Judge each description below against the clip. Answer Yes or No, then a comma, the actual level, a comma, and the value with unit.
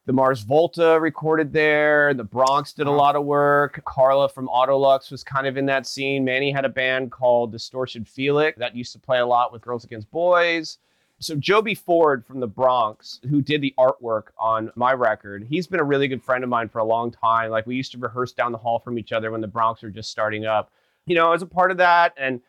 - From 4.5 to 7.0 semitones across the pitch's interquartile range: No, average, 3.7 semitones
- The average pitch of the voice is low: Yes, low, 130 Hz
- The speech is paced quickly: Yes, fast, 240 wpm